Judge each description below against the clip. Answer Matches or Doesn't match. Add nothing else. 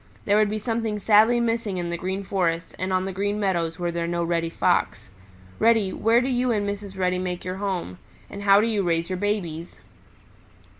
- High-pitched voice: Matches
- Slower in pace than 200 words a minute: Doesn't match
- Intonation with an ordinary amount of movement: Matches